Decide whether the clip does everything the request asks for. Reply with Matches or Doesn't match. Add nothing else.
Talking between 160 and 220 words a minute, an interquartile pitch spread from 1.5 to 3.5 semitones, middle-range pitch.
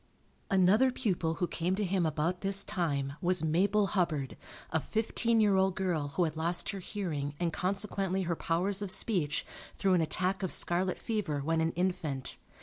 Matches